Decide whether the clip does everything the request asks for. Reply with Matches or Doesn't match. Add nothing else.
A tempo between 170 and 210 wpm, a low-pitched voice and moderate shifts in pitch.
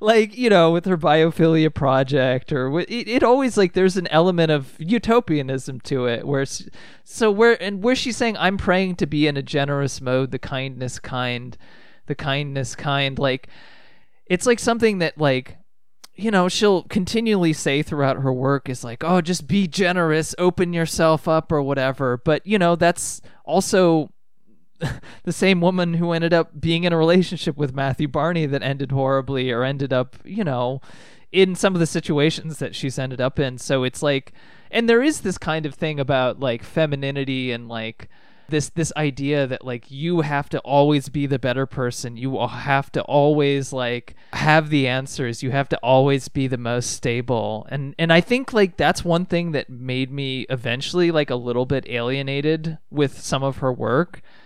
Doesn't match